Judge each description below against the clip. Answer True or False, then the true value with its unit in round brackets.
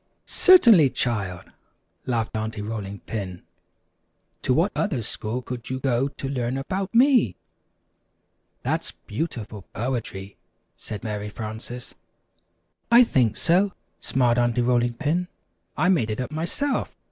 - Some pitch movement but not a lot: False (6.1 semitones)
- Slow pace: True (125 wpm)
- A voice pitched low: True (120 Hz)